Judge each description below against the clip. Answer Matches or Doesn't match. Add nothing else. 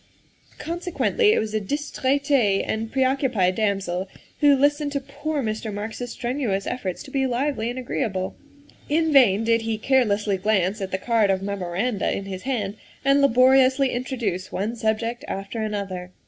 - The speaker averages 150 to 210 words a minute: Matches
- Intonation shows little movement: Doesn't match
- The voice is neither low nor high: Doesn't match